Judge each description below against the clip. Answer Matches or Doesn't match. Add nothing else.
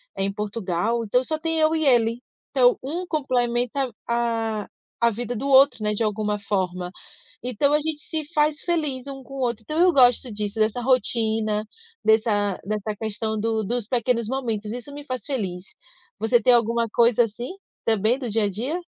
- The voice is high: Matches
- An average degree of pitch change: Matches